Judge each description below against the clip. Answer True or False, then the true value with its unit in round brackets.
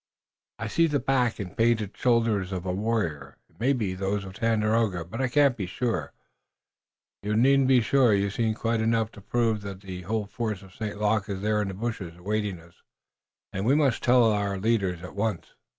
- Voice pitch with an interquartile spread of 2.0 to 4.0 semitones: True (3.2 semitones)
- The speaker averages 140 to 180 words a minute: False (200 wpm)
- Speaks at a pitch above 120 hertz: False (105 Hz)